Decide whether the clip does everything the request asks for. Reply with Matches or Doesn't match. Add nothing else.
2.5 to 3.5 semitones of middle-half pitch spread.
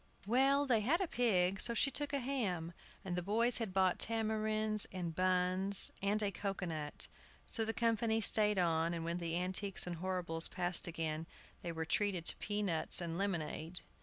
Doesn't match